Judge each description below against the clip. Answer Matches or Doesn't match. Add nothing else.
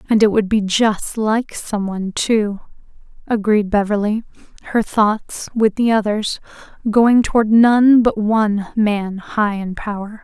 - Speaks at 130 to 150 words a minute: Matches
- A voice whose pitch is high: Matches